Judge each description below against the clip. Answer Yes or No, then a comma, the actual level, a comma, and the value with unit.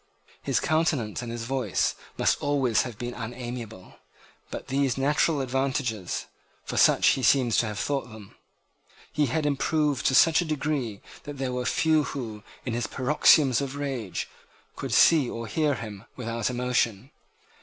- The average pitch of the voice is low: Yes, low, 130 Hz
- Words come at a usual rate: Yes, average, 155 wpm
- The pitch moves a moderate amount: Yes, average, 3.7 semitones